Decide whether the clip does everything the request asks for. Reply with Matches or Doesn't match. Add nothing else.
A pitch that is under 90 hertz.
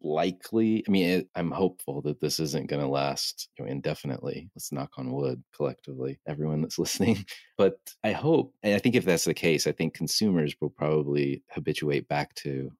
Matches